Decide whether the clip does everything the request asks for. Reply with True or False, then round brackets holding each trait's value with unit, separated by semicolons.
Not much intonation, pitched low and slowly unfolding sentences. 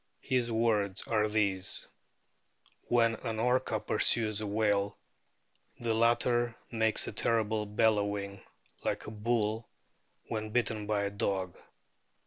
True (2.0 semitones; 110 Hz; 115 wpm)